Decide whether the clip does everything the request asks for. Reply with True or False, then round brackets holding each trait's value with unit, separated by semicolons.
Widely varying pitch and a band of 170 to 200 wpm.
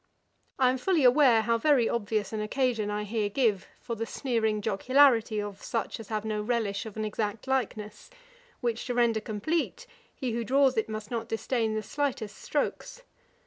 False (3.0 semitones; 180 wpm)